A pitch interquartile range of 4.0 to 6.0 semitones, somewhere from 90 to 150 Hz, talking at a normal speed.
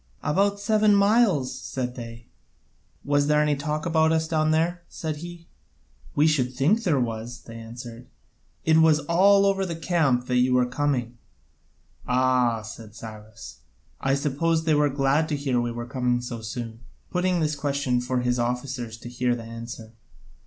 Yes: average, 4.7 semitones; low, 135 Hz; average, 165 wpm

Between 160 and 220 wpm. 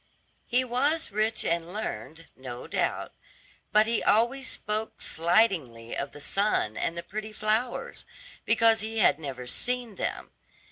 No: average, 140 wpm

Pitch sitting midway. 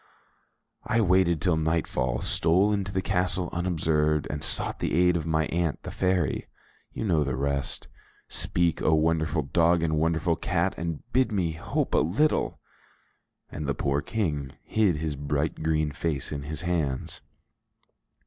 No: very low, 80 Hz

